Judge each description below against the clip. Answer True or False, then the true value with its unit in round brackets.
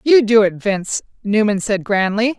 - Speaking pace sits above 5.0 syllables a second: False (4.8 syllables/s)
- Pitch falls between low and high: False (210 Hz)